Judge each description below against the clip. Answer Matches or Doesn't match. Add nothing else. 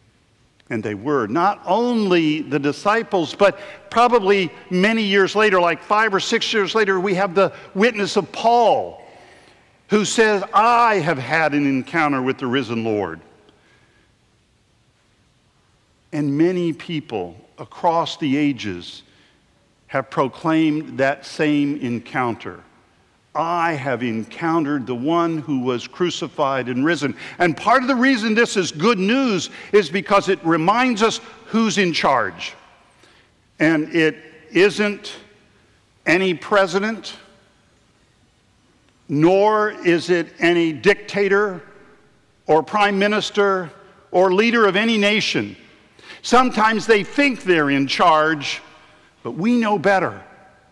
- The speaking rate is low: Matches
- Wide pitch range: Matches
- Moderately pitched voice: Matches